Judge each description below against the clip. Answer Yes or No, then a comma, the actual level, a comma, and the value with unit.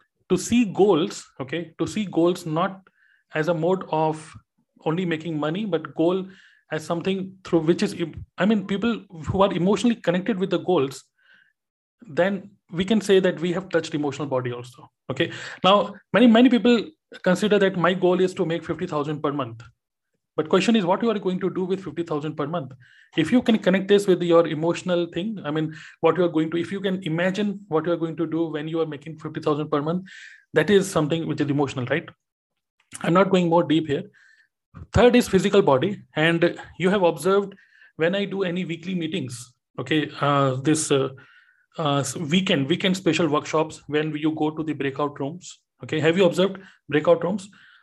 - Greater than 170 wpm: Yes, fast, 190 wpm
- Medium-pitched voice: Yes, medium, 170 Hz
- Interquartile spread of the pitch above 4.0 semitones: No, average, 3.6 semitones